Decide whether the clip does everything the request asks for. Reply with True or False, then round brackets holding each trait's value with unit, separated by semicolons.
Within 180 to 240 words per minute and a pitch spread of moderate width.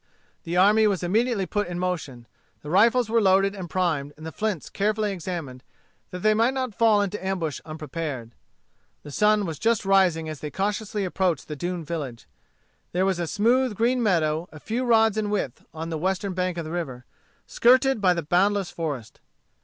True (185 wpm; 4.6 semitones)